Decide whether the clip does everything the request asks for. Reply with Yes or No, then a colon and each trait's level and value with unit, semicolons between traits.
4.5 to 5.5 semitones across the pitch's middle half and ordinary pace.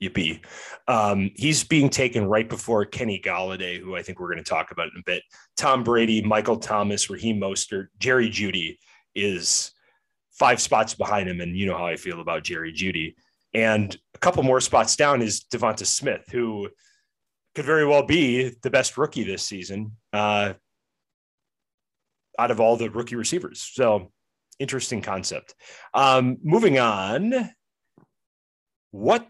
Yes: average, 4.9 semitones; average, 155 wpm